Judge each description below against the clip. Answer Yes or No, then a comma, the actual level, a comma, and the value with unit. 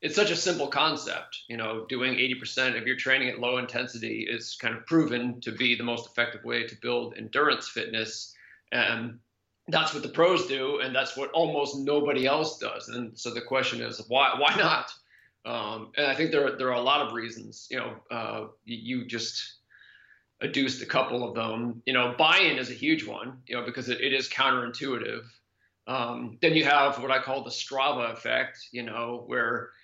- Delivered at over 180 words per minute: Yes, average, 200 wpm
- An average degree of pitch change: No, narrow, 2.3 semitones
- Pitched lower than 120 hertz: No, low, 125 Hz